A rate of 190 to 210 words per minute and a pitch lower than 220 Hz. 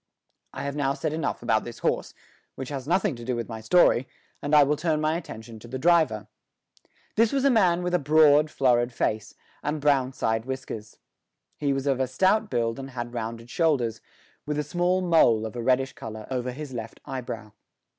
Yes: average, 200 wpm; low, 135 Hz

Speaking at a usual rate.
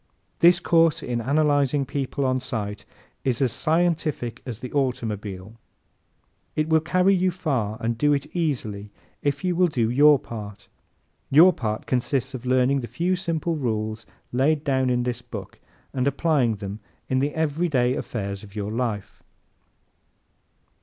Yes: average, 155 wpm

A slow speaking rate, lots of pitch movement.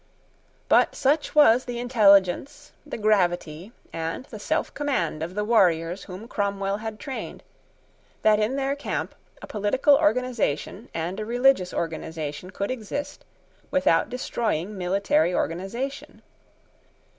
Yes: slow, 120 wpm; wide, 6.0 semitones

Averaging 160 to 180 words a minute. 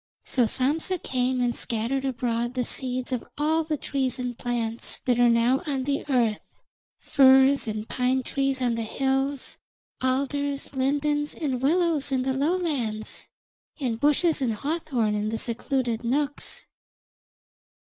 No: average, 140 wpm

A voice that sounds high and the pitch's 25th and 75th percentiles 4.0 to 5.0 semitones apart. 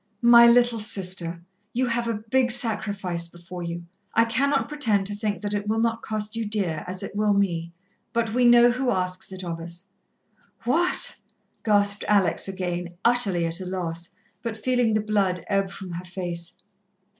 Yes: high, 205 Hz; average, 4.3 semitones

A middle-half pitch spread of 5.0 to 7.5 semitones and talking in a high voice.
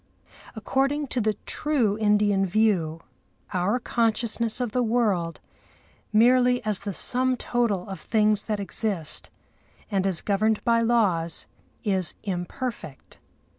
No: average, 3.6 semitones; high, 215 Hz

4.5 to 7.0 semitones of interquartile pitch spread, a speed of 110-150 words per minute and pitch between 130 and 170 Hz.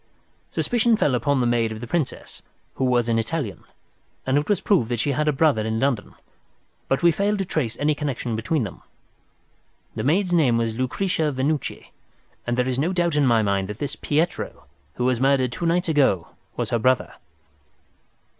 No: average, 5.1 semitones; average, 190 wpm; low, 135 Hz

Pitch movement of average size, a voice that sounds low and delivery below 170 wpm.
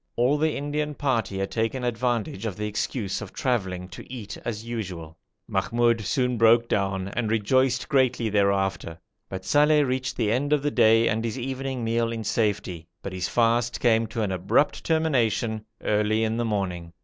No: average, 3.7 semitones; low, 115 Hz; average, 175 wpm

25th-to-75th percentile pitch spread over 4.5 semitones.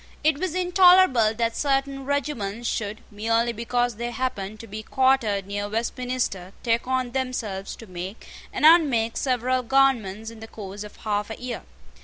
No: average, 3.8 semitones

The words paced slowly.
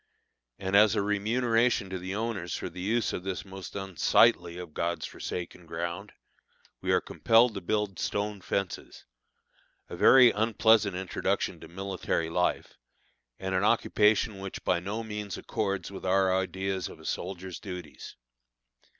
No: average, 150 wpm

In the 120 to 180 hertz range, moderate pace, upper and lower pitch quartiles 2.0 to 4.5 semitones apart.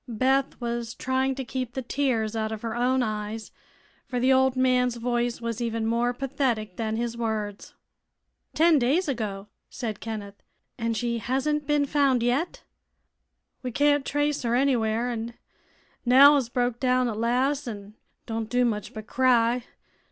No: high, 245 Hz; average, 160 wpm; average, 2.7 semitones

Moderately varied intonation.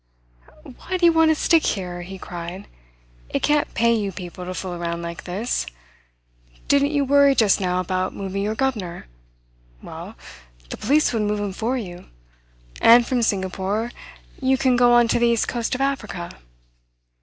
No: wide, 5.9 semitones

